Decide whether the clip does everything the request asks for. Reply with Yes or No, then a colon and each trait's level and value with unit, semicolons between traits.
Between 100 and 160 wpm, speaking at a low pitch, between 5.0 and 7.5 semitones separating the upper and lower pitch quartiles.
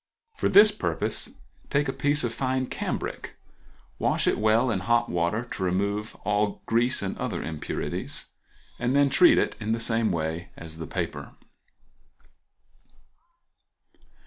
Yes: average, 140 wpm; low, 115 Hz; average, 5.3 semitones